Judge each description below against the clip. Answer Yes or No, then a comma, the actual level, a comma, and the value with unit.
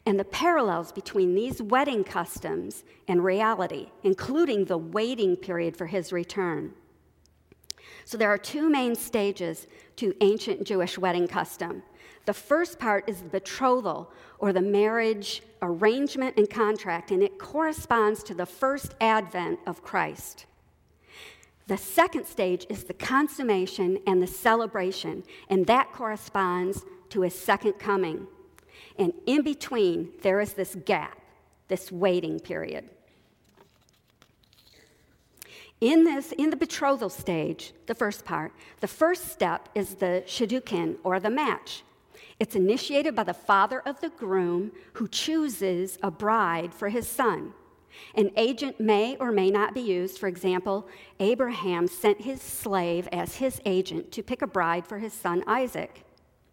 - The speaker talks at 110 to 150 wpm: Yes, average, 140 wpm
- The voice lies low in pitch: No, high, 205 Hz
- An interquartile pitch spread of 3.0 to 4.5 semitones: No, wide, 5.4 semitones